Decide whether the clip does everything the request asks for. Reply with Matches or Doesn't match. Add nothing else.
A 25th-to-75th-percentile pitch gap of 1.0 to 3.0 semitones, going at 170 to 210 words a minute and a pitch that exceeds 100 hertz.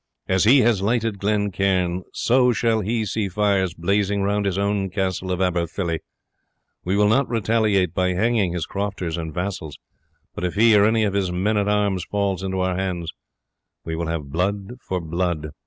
Doesn't match